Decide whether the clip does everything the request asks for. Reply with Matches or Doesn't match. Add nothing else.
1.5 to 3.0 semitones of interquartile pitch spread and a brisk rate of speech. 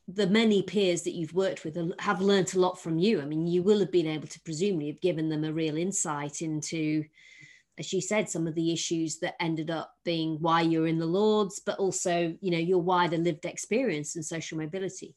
Matches